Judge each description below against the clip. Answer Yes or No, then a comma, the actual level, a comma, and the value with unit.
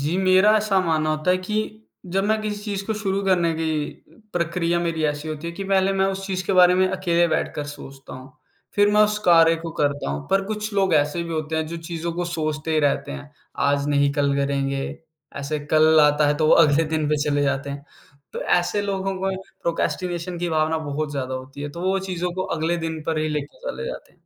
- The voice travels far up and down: No, average, 4.0 semitones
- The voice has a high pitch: No, medium, 165 Hz